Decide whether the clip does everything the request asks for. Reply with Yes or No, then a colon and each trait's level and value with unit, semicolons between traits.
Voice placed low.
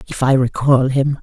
Yes: low, 130 Hz